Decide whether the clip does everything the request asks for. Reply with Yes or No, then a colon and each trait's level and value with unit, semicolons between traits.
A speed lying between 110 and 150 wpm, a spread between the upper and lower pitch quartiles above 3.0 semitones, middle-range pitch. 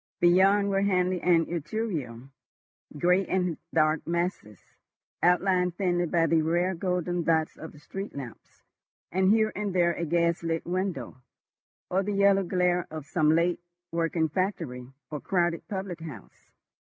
No: average, 140 wpm; narrow, 2.5 semitones; medium, 175 Hz